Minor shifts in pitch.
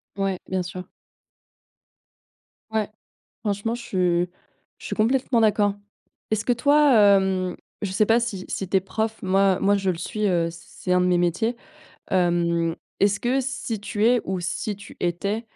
No: average, 3.4 semitones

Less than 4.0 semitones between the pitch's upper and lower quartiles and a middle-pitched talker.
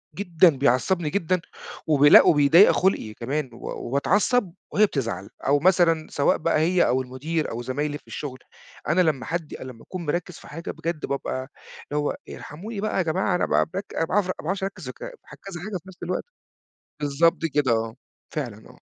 No: average, 4.7 semitones; medium, 160 Hz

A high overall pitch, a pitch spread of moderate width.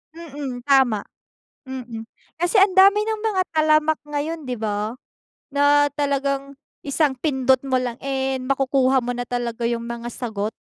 Yes: very high, 270 Hz; average, 3.2 semitones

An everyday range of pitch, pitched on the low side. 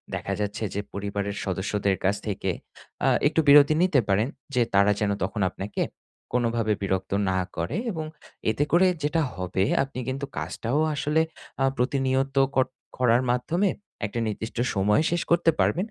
No: wide, 5.9 semitones; low, 115 Hz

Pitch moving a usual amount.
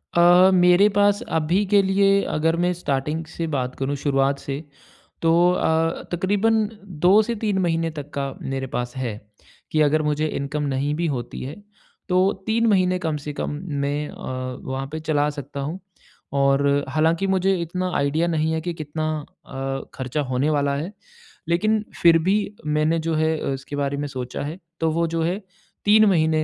Yes: average, 4.1 semitones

